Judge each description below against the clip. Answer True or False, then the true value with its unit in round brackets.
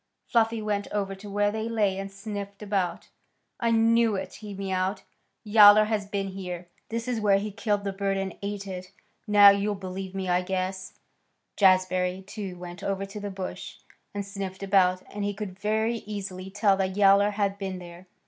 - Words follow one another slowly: False (185 wpm)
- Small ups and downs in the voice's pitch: True (1.6 semitones)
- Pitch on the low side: False (200 Hz)